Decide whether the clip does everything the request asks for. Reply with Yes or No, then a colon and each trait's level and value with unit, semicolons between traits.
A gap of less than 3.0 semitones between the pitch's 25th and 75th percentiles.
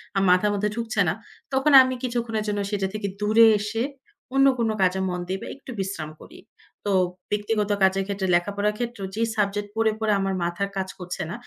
Yes: narrow, 2.5 semitones